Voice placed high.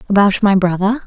Yes: high, 200 Hz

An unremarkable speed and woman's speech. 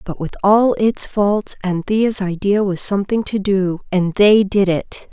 Yes: average, 175 wpm; female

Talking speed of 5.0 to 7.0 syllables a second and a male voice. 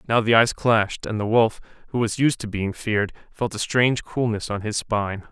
Yes: 5.4 syllables/s; male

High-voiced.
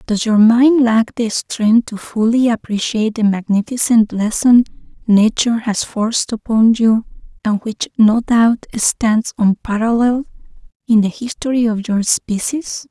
Yes: high, 225 Hz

